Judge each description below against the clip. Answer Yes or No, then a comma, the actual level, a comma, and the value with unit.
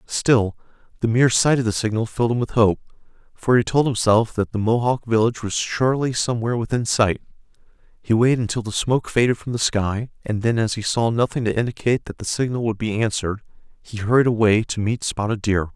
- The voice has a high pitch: No, low, 115 Hz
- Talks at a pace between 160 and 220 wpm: Yes, fast, 205 wpm